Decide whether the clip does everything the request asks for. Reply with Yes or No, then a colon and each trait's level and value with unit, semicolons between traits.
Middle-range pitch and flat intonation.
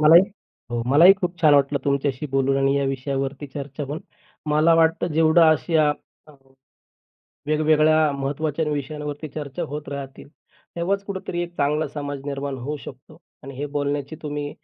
Yes: medium, 145 Hz; narrow, 2.2 semitones